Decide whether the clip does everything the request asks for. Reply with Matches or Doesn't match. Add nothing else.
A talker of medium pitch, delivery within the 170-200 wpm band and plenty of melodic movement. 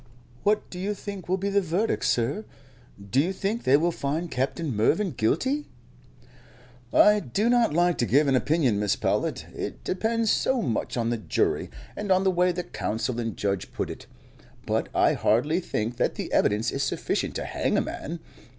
Matches